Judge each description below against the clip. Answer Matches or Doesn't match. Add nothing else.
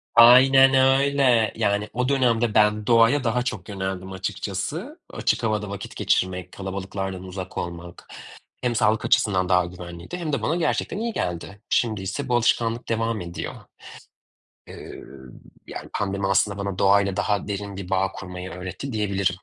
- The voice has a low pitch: Matches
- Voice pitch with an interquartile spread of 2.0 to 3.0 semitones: Doesn't match